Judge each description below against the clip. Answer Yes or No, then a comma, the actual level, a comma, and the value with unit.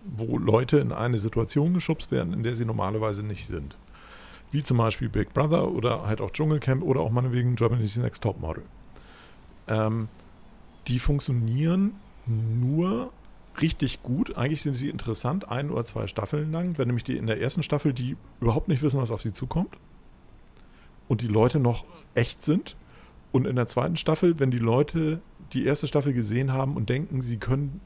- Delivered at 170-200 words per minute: Yes, average, 175 wpm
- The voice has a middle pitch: No, low, 125 Hz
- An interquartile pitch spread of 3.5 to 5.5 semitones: Yes, average, 4.7 semitones